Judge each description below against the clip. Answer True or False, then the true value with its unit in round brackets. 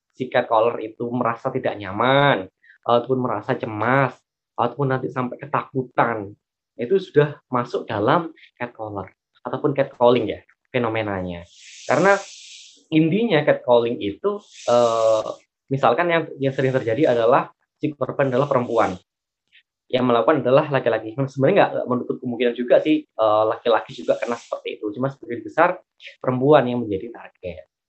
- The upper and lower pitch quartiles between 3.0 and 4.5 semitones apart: True (3.4 semitones)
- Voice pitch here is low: True (125 Hz)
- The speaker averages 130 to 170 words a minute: True (135 wpm)